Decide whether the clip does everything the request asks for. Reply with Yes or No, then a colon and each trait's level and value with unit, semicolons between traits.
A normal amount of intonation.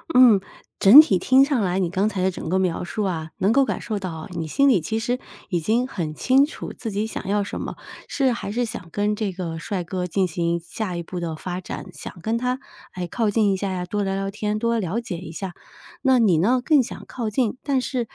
Yes: average, 4.6 semitones